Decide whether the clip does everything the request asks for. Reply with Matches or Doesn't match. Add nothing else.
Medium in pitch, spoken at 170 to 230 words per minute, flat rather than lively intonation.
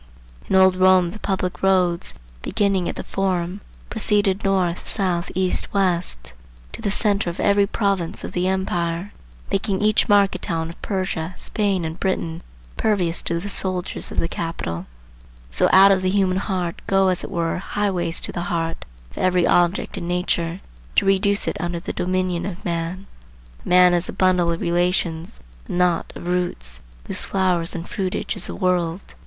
Matches